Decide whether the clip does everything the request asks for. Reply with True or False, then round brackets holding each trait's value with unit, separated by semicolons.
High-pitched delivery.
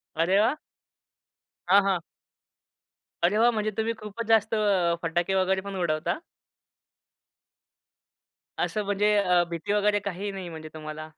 True (195 Hz)